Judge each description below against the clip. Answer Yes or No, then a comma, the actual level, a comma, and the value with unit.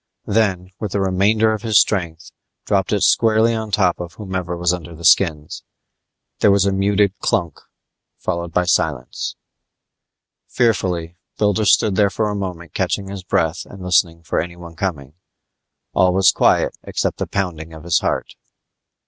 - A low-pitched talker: Yes, very low, 95 Hz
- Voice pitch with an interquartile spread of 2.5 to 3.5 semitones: Yes, average, 3.1 semitones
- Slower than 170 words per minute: Yes, average, 155 wpm